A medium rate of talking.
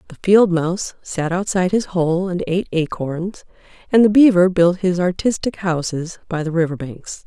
Yes: average, 175 wpm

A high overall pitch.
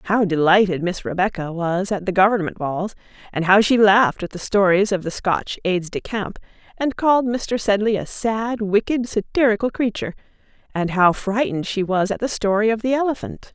Yes: high, 205 Hz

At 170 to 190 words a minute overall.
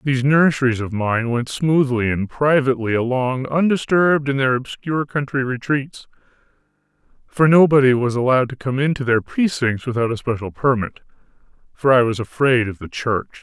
No: average, 150 wpm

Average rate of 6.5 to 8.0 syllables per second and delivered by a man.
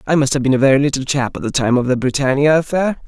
Yes: 7.0 syllables/s; male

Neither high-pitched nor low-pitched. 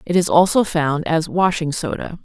Yes: medium, 165 Hz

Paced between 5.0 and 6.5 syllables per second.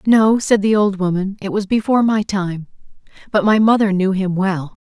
Yes: 5.1 syllables/s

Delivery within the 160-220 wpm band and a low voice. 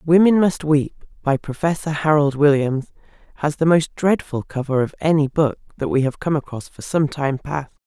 No: average, 185 wpm; medium, 150 Hz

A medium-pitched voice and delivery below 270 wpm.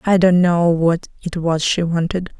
Yes: medium, 175 Hz; average, 200 wpm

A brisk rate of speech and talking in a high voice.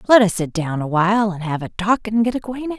Yes: fast, 280 wpm; high, 200 Hz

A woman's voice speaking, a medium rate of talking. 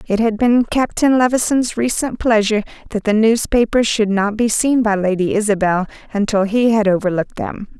Yes: female; average, 175 wpm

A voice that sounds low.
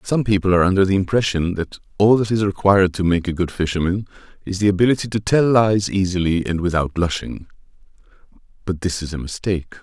Yes: very low, 95 Hz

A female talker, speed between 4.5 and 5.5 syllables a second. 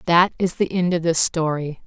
Yes: female; 4.9 syllables/s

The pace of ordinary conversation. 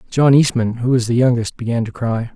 No: fast, 230 wpm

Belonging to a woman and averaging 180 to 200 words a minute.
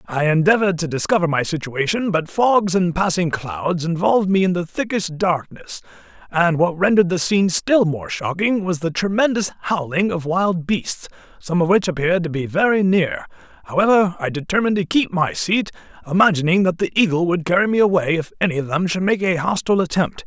No: male; average, 190 wpm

